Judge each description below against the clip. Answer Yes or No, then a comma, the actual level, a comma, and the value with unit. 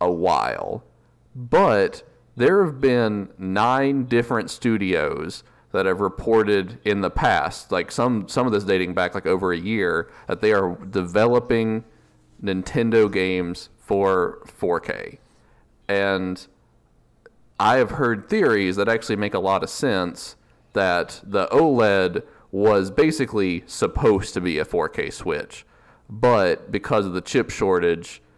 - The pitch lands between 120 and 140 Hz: No, low, 105 Hz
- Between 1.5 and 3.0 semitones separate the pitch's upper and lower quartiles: No, average, 4.0 semitones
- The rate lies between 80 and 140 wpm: Yes, slow, 135 wpm